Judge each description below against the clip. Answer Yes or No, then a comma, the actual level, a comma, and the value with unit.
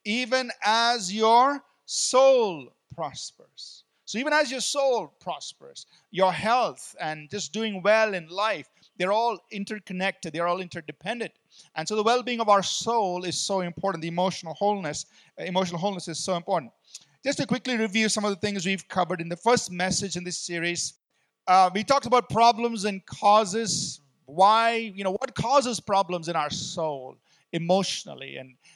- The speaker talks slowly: No, average, 165 wpm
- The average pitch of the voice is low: No, high, 200 Hz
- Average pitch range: Yes, average, 4.3 semitones